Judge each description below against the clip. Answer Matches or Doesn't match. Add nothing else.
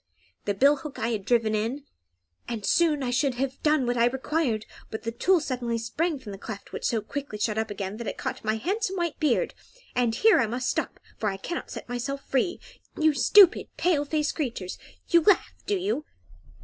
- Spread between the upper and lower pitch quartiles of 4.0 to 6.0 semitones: Matches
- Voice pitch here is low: Doesn't match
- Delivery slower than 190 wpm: Doesn't match